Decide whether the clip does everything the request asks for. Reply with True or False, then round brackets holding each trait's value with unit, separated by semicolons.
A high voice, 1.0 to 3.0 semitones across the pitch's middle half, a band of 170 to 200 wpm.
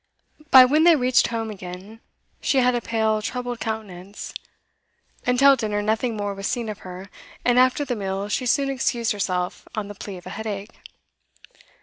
False (220 Hz; 3.7 semitones; 175 wpm)